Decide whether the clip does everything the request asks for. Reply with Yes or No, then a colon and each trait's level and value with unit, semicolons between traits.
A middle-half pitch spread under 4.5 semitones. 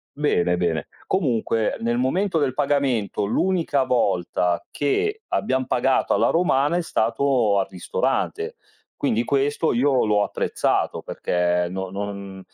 No: wide, 6.5 semitones